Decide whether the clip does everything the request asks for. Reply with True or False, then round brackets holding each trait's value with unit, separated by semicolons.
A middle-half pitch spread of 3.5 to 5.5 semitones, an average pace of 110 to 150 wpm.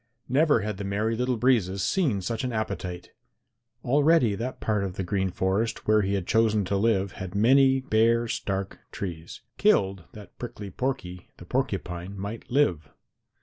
False (4.1 semitones; 160 wpm)